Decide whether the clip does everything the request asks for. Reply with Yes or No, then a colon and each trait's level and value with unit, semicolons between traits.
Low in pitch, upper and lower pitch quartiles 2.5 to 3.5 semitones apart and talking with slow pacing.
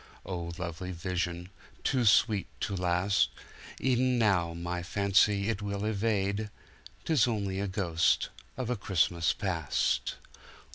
Yes: low, 100 Hz; average, 3.2 semitones; slow, 115 wpm